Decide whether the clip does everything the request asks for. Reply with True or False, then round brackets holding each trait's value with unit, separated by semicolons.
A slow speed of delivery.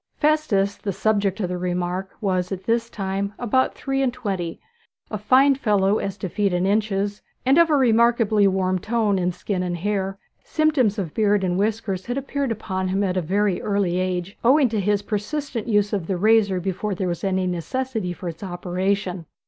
False (190 wpm)